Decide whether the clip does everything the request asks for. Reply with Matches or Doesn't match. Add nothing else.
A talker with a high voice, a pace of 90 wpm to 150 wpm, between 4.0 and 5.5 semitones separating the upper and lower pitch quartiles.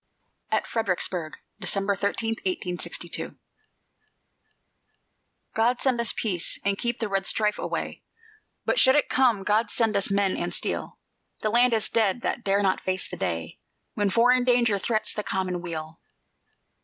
Doesn't match